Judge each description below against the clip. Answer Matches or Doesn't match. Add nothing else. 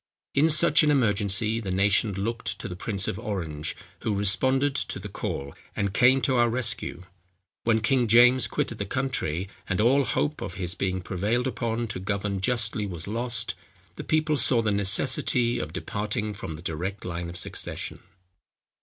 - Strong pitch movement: Doesn't match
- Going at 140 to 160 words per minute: Doesn't match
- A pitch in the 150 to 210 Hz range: Doesn't match